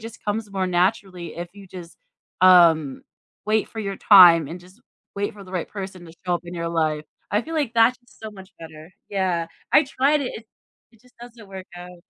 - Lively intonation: No, average, 3.9 semitones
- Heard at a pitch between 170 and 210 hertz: Yes, high, 190 Hz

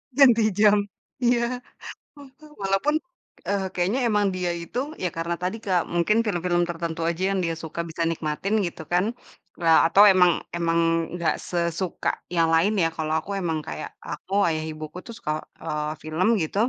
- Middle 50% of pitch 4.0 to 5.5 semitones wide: No, average, 3.2 semitones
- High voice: No, medium, 175 Hz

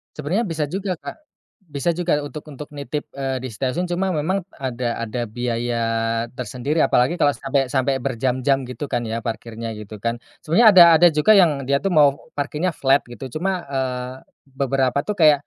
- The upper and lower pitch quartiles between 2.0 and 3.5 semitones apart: No, average, 4.1 semitones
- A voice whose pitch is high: No, medium, 140 Hz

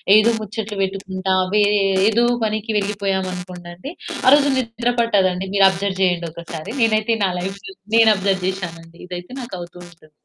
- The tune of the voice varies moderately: Yes, average, 3.4 semitones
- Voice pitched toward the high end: Yes, high, 195 Hz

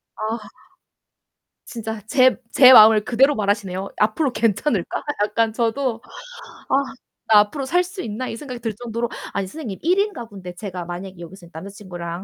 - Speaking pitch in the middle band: No, high, 220 Hz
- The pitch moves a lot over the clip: No, average, 4.4 semitones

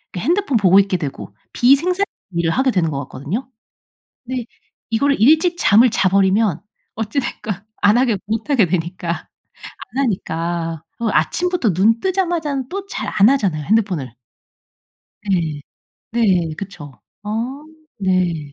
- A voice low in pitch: No, high, 205 Hz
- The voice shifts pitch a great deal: Yes, wide, 7.3 semitones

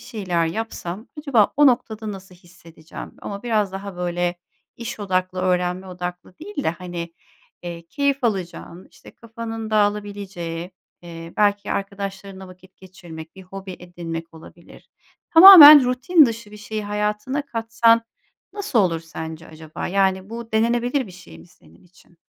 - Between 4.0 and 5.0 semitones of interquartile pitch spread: Yes, average, 4.3 semitones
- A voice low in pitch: No, high, 195 Hz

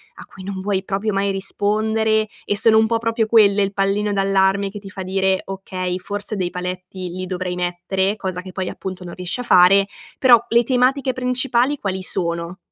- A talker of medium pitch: No, high, 195 Hz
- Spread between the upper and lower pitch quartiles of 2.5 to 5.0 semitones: Yes, average, 2.8 semitones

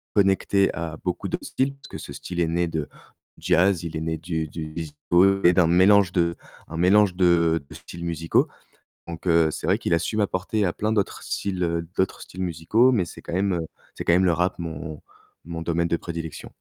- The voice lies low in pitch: Yes, very low, 85 Hz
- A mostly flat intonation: Yes, narrow, 2.3 semitones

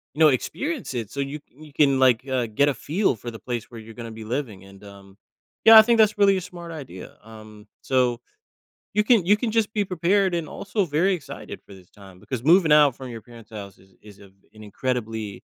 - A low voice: Yes, low, 130 Hz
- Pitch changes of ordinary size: No, wide, 8.0 semitones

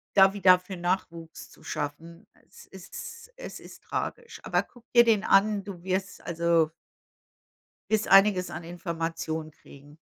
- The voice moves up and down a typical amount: Yes, average, 3.1 semitones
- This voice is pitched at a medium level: Yes, medium, 180 Hz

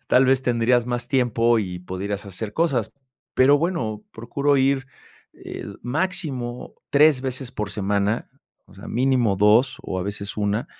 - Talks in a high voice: No, low, 120 Hz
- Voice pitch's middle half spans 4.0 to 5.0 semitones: Yes, average, 4.3 semitones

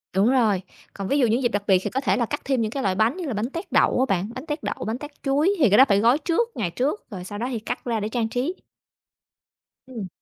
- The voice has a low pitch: No, high, 240 Hz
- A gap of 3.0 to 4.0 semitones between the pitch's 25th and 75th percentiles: No, average, 4.7 semitones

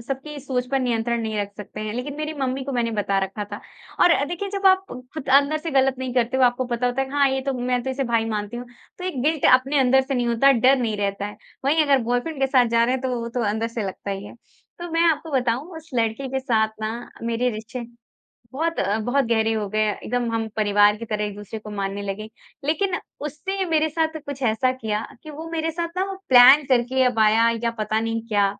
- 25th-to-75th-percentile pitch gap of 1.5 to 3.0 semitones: No, average, 4.1 semitones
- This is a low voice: No, very high, 250 Hz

